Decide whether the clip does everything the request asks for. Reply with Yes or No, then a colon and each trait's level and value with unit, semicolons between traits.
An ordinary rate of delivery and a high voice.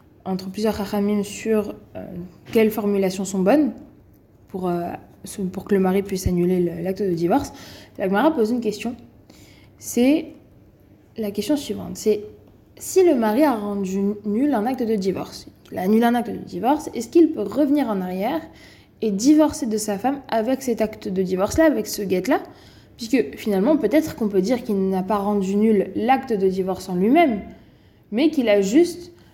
Yes: average, 180 wpm; high, 210 Hz